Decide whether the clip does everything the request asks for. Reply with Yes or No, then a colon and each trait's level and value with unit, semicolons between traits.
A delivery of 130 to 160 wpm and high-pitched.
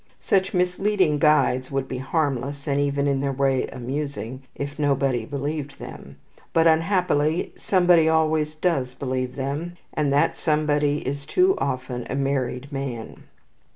No: average, 140 wpm; medium, 140 Hz